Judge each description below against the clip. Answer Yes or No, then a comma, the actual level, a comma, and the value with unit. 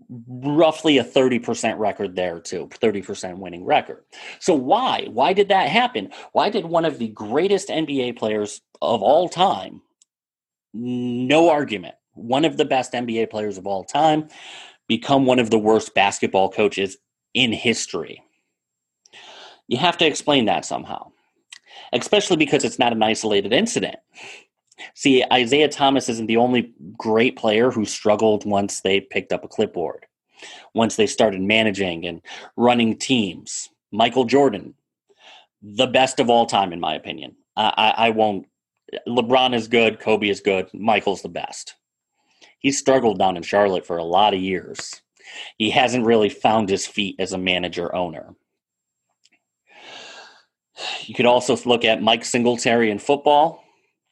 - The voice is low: Yes, low, 115 Hz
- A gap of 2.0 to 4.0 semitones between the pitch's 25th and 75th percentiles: No, average, 4.6 semitones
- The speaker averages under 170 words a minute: Yes, average, 150 wpm